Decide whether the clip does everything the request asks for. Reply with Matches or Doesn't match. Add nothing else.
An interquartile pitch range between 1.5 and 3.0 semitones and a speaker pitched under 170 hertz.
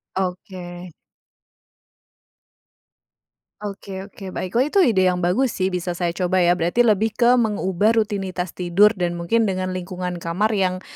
Doesn't match